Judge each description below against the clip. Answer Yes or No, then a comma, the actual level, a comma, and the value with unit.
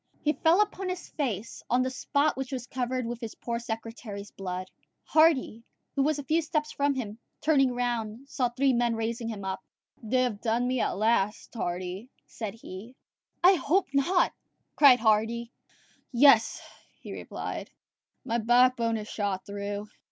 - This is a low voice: No, high, 240 Hz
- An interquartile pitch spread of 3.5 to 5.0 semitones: Yes, average, 3.8 semitones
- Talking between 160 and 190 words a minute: Yes, average, 165 wpm